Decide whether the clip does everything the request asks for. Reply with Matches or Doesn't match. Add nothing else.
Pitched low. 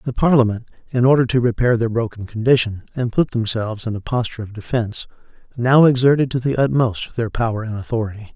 Matches